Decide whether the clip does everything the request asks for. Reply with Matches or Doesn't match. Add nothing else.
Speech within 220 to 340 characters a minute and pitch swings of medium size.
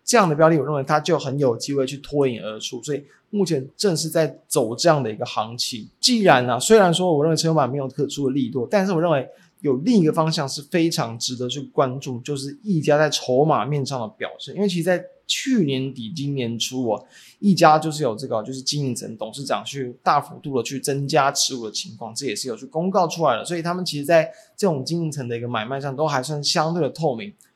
Doesn't match